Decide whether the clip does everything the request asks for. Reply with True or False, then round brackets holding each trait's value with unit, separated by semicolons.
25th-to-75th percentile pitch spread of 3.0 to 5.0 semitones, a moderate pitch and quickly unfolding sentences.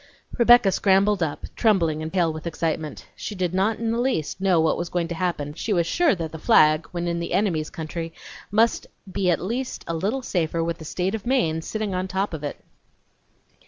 True (4.2 semitones; 180 Hz; 215 wpm)